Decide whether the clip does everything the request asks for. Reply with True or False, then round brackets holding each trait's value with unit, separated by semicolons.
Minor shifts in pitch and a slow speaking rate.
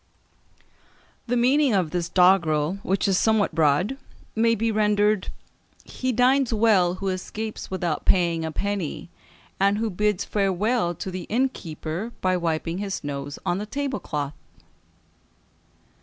False (4.2 semitones; 130 wpm)